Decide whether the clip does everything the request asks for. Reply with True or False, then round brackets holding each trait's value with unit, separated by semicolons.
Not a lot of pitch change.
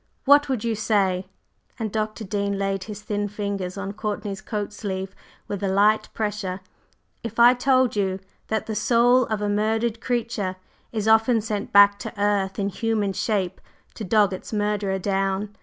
True (2.0 semitones)